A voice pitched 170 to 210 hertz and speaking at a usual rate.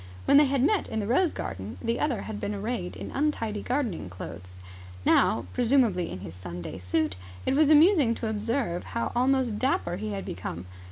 No: high, 220 Hz; average, 185 wpm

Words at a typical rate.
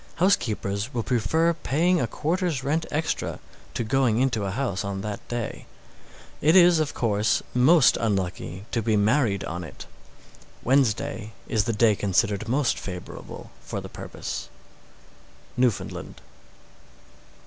No: slow, 130 wpm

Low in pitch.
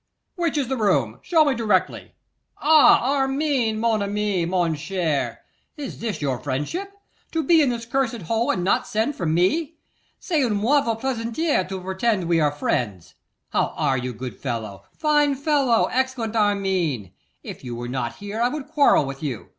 No: high, 215 Hz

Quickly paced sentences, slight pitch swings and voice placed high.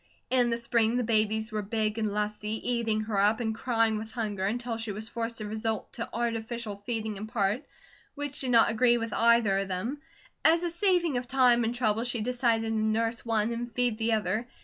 Yes: fast, 210 wpm; narrow, 1.9 semitones; high, 225 Hz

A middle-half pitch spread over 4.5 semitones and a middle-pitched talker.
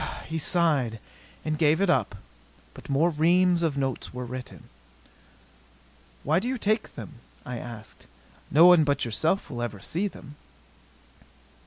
Yes: wide, 5.5 semitones; medium, 155 Hz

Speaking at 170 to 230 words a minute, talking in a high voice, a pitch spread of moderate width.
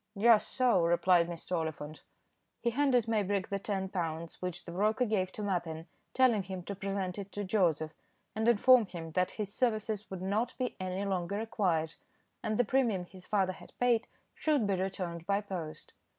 Yes: average, 180 wpm; high, 195 Hz; average, 3.5 semitones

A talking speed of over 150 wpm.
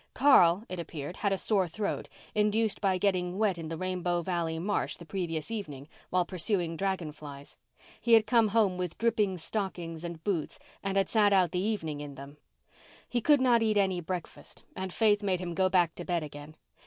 Yes: average, 195 wpm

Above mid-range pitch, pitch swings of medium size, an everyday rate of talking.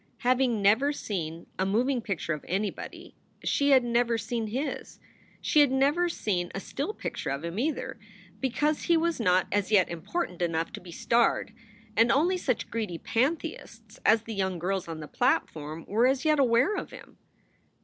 No: high, 230 Hz; wide, 6.5 semitones; average, 175 wpm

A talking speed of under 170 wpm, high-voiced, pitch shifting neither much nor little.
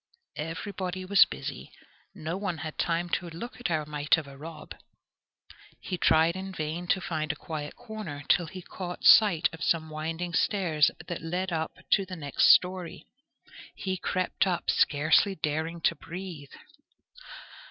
No: average, 155 wpm; medium, 170 Hz; average, 3.0 semitones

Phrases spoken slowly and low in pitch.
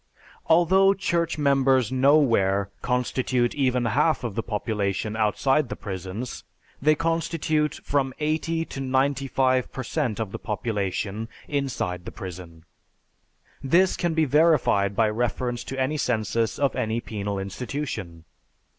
Yes: slow, 130 wpm; low, 125 Hz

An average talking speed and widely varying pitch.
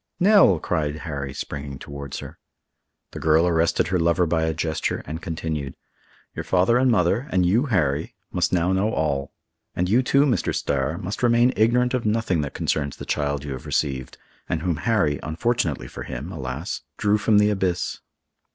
Yes: average, 170 wpm; wide, 6.4 semitones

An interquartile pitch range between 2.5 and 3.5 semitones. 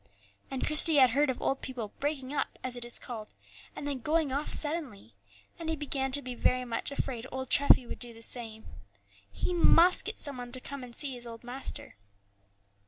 Yes: average, 3.0 semitones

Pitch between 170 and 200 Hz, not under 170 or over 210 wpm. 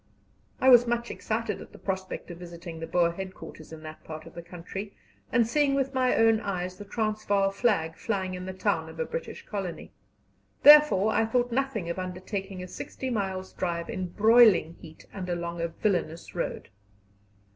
Yes: high, 190 Hz; average, 180 wpm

